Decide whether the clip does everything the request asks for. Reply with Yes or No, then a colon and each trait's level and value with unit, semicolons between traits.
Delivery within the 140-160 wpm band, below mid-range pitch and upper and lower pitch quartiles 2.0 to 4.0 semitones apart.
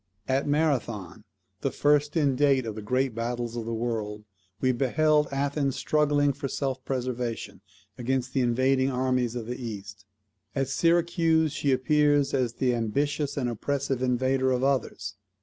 Yes: average, 150 wpm; low, 130 Hz; average, 3.0 semitones